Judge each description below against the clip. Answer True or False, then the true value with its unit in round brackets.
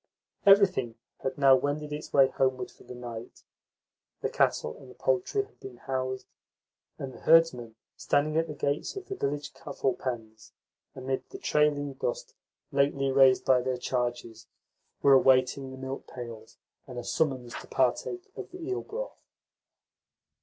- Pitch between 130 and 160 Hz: True (135 Hz)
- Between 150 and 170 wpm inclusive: True (155 wpm)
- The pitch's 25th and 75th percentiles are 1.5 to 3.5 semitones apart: True (2.9 semitones)